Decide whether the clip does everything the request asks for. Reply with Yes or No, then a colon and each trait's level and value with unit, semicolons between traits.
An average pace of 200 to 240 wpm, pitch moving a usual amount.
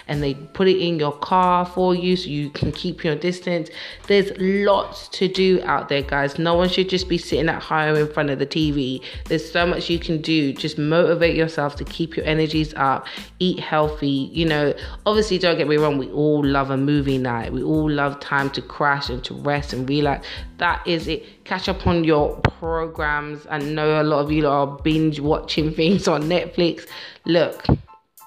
Yes: fast, 205 wpm; average, 3.1 semitones